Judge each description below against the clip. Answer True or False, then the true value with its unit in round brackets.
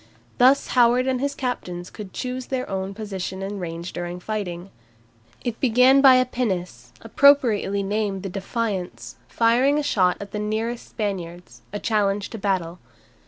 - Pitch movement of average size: True (4.7 semitones)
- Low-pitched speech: False (210 Hz)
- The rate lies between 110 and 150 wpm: False (160 wpm)